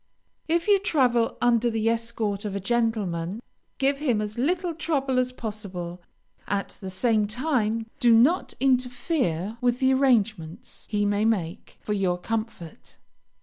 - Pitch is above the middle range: Yes, high, 230 Hz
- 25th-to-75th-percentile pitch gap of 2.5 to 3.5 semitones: No, average, 4.0 semitones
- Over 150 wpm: No, average, 145 wpm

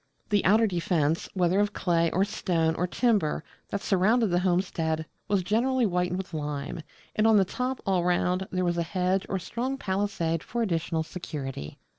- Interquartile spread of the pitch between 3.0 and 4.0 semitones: Yes, average, 3.5 semitones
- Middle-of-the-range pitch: Yes, medium, 180 Hz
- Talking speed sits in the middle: Yes, average, 175 wpm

